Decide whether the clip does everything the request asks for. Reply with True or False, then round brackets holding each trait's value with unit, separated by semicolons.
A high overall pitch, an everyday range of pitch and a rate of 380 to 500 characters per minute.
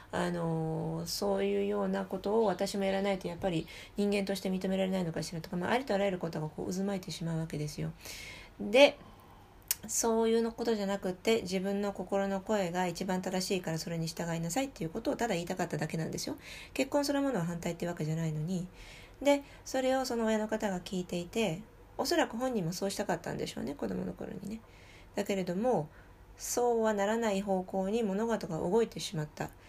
True (195 Hz; 4.6 semitones; 430 characters per minute)